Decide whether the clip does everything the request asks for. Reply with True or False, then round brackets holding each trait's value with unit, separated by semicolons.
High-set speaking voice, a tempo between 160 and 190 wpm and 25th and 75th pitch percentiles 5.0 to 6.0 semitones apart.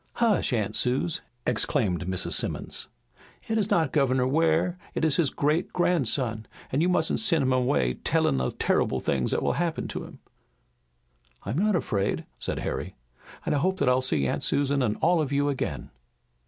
False (140 Hz; 180 wpm; 5.3 semitones)